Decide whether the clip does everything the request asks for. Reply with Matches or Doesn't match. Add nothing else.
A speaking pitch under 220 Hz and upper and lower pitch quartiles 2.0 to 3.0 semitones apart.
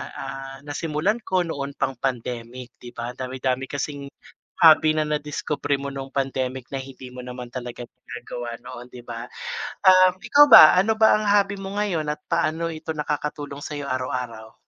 Doesn't match